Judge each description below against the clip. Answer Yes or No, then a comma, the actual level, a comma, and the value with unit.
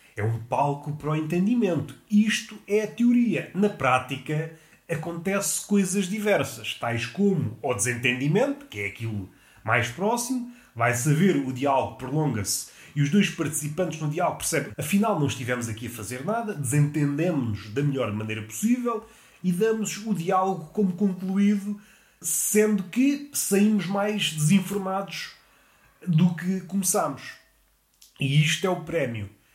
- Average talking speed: Yes, average, 135 wpm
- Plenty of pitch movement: Yes, wide, 7.2 semitones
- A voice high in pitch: No, medium, 165 Hz